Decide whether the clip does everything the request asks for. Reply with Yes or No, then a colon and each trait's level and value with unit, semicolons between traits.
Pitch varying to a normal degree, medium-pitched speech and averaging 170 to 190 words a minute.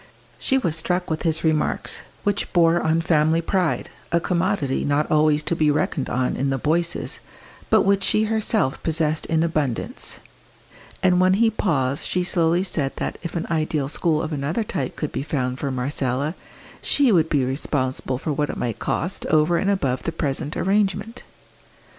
Yes: average, 3.8 semitones; medium, 160 Hz; average, 175 wpm